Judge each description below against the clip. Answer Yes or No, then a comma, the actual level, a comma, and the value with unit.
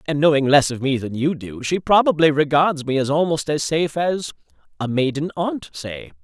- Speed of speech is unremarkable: Yes, average, 190 wpm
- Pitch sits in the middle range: Yes, medium, 150 Hz